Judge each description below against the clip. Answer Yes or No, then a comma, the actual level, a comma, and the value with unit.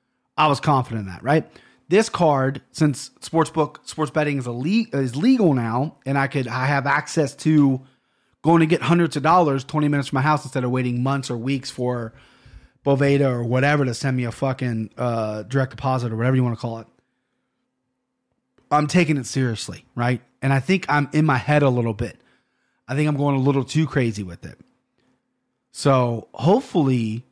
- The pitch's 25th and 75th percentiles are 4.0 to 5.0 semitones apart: No, average, 3.2 semitones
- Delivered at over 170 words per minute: Yes, average, 195 wpm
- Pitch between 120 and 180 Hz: Yes, low, 135 Hz